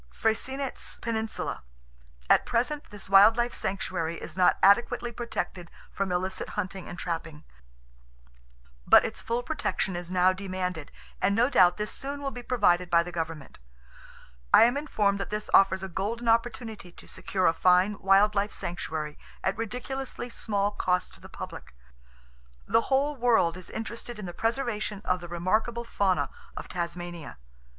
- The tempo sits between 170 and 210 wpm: No, average, 155 wpm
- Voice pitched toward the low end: No, high, 195 Hz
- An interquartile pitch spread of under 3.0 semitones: No, average, 4.7 semitones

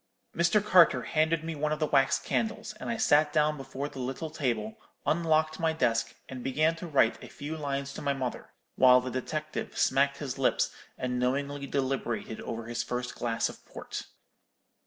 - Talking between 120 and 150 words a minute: No, average, 180 wpm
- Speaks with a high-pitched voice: No, medium, 140 Hz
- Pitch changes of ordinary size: Yes, average, 3.6 semitones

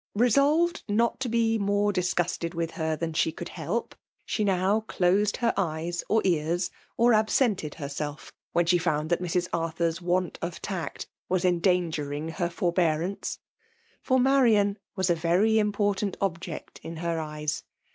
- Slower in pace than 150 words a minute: No, average, 155 wpm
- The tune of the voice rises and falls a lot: No, average, 3.9 semitones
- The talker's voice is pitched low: No, medium, 180 Hz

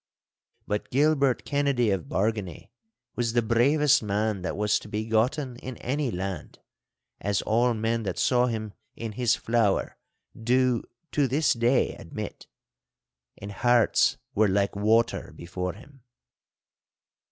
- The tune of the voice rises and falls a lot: No, average, 3.4 semitones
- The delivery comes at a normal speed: No, slow, 130 wpm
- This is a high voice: No, low, 115 Hz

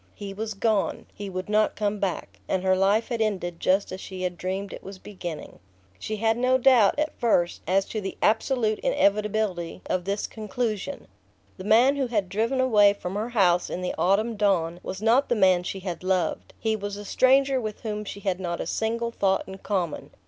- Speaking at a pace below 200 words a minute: No, fast, 205 wpm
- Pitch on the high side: Yes, high, 205 Hz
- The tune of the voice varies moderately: Yes, average, 3.0 semitones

